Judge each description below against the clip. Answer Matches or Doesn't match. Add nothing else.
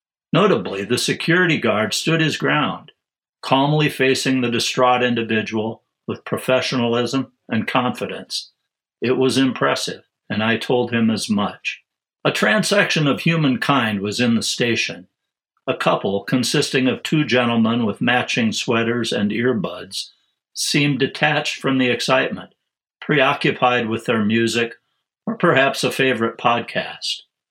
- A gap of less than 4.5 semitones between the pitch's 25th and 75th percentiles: Matches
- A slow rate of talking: Matches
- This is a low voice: Matches